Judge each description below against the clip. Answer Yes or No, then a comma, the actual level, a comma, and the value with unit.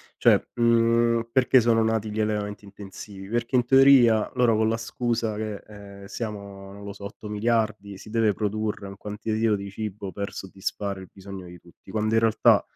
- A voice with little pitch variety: Yes, narrow, 2.2 semitones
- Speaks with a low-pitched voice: Yes, low, 105 Hz